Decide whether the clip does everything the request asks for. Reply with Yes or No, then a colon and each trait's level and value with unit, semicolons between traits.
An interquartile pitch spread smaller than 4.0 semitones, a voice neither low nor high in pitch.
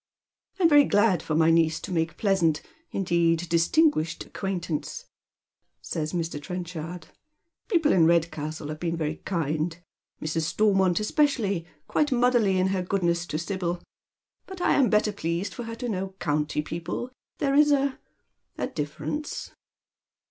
No: wide, 5.4 semitones; medium, 180 Hz